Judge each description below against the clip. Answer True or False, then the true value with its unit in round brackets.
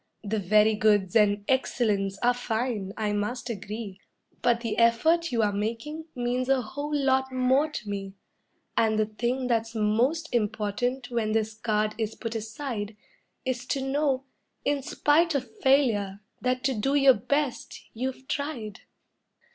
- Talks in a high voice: True (235 Hz)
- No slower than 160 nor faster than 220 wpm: False (150 wpm)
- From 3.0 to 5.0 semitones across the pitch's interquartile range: True (3.8 semitones)